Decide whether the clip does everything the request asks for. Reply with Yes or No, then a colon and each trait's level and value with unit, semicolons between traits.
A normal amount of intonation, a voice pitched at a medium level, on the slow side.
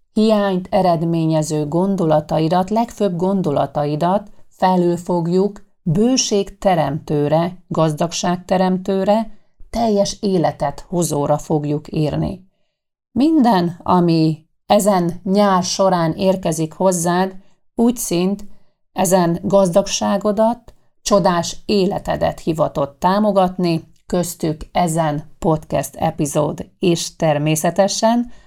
Yes: average, 3.6 semitones; medium, 180 Hz; slow, 75 wpm